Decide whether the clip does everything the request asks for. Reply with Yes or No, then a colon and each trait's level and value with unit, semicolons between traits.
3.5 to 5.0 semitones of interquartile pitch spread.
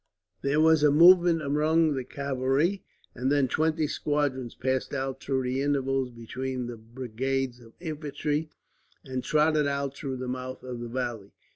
No: average, 2.8 semitones